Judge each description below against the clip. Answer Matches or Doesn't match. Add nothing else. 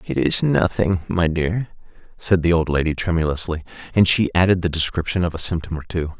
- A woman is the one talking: Doesn't match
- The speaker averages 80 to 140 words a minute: Doesn't match